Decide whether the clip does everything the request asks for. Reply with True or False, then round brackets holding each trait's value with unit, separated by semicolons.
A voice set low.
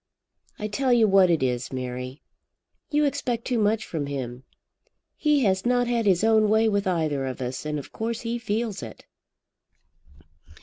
False (205 Hz)